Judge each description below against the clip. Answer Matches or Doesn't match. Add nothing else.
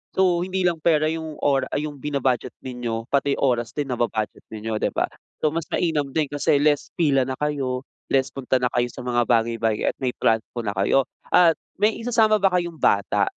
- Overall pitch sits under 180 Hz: Matches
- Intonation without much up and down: Doesn't match